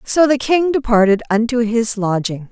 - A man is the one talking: No, female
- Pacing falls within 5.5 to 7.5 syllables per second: No, 4.7 syllables/s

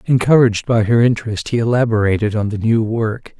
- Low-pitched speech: Yes, low, 115 Hz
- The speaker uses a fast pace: No, average, 175 wpm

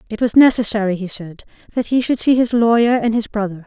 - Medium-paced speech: No, fast, 230 wpm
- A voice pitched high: Yes, high, 220 Hz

